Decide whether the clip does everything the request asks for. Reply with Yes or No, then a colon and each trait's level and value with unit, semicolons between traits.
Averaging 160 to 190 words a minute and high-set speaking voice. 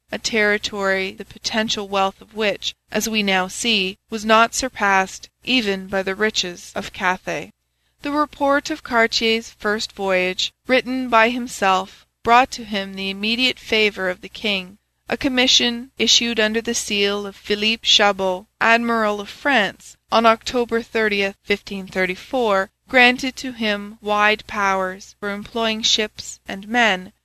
No: average, 145 wpm; high, 215 Hz